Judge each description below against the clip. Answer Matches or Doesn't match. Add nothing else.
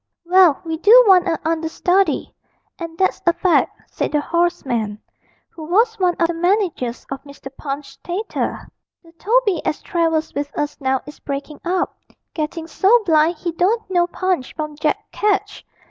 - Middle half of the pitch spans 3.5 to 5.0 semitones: Matches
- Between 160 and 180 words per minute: Matches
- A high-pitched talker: Matches